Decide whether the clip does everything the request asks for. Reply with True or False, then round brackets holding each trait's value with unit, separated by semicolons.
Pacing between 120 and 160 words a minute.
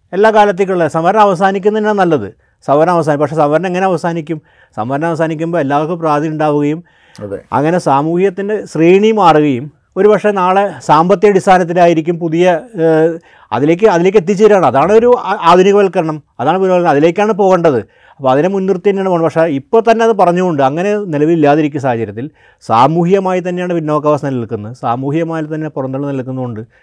True (125 wpm)